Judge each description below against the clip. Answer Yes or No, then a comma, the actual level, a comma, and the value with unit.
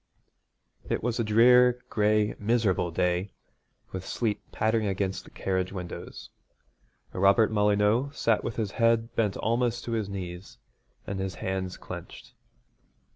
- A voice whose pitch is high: No, low, 105 Hz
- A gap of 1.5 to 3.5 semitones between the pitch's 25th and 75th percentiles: Yes, average, 3.2 semitones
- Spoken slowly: Yes, slow, 130 wpm